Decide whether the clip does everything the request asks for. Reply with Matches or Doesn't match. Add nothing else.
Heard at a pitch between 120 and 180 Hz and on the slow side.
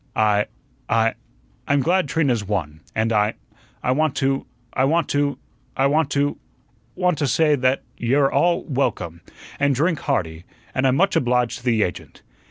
Doesn't match